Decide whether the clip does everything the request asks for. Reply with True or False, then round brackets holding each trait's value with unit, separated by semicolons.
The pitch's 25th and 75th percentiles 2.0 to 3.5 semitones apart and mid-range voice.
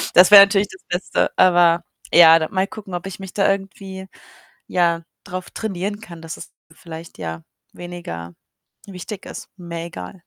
True (2.4 semitones; 180 Hz)